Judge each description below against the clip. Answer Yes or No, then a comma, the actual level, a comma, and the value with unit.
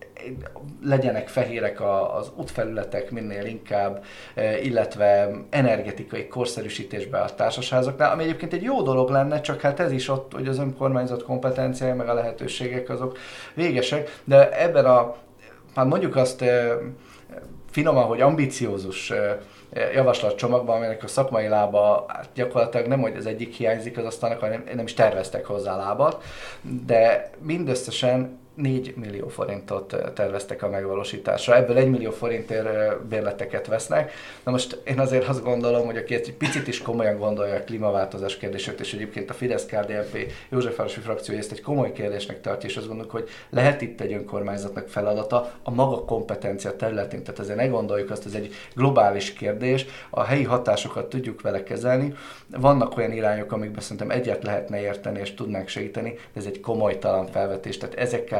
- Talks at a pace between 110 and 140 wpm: No, average, 150 wpm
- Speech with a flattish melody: No, average, 3.6 semitones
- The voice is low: Yes, low, 120 Hz